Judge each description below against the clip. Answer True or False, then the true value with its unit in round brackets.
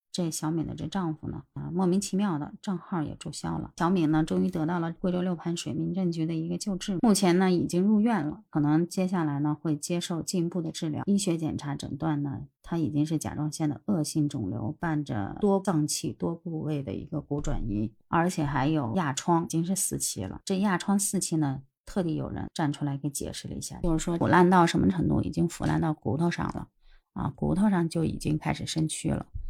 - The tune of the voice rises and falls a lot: False (3.1 semitones)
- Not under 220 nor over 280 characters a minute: False (325 characters per minute)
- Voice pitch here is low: False (160 Hz)